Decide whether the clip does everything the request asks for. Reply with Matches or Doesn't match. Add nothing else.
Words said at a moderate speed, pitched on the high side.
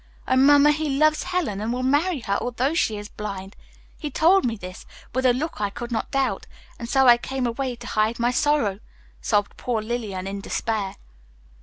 Matches